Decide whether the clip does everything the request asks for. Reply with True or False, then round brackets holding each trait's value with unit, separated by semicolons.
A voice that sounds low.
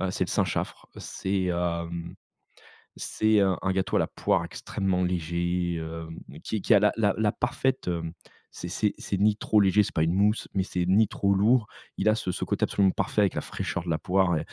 True (95 Hz)